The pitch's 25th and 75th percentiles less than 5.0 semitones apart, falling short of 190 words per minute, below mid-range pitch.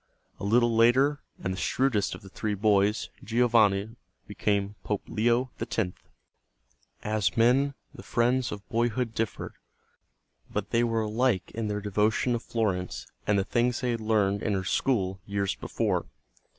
Yes: average, 2.8 semitones; average, 150 wpm; low, 110 Hz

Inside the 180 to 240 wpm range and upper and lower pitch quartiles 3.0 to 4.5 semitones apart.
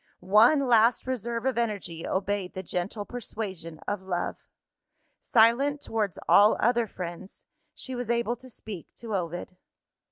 No: slow, 135 wpm; average, 4.0 semitones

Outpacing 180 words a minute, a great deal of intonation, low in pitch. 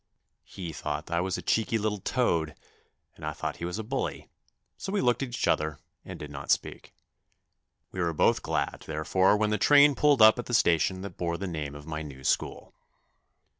Yes: fast, 205 wpm; wide, 6.3 semitones; very low, 95 Hz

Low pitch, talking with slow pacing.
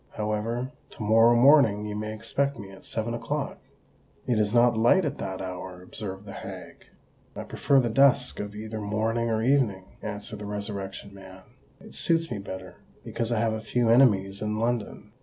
No: low, 110 Hz; average, 175 wpm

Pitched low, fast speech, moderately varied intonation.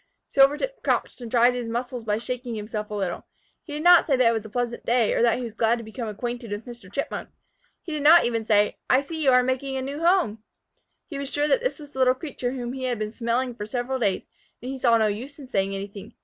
No: high, 245 Hz; fast, 255 wpm; average, 3.4 semitones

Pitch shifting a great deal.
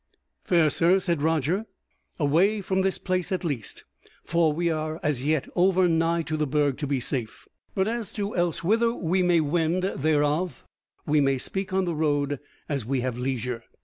No: average, 4.2 semitones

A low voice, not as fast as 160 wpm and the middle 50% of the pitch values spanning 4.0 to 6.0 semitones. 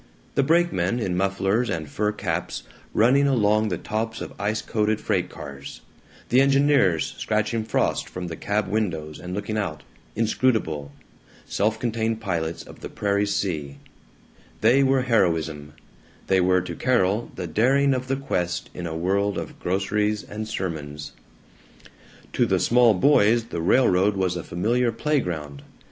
Yes: low, 105 Hz; average, 150 wpm; average, 4.7 semitones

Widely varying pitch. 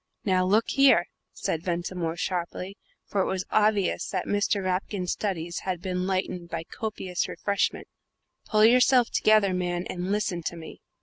No: narrow, 2.6 semitones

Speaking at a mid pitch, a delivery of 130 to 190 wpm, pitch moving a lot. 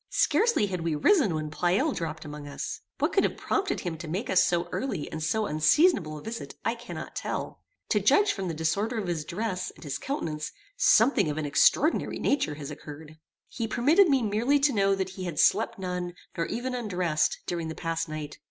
No: medium, 180 Hz; fast, 205 wpm; wide, 6.7 semitones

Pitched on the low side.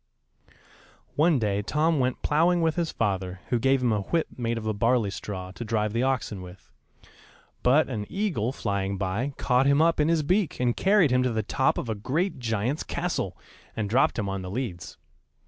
Yes: low, 120 Hz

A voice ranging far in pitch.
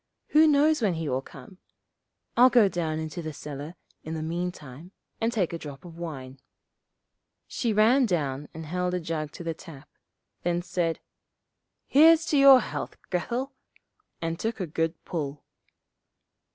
Yes: wide, 6.0 semitones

